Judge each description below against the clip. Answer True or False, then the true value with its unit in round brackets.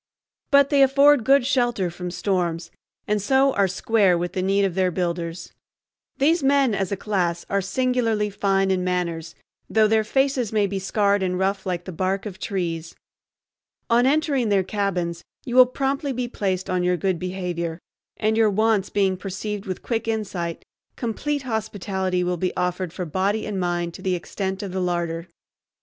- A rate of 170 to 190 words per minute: True (175 wpm)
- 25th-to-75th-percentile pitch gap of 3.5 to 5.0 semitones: True (3.8 semitones)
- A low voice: False (195 Hz)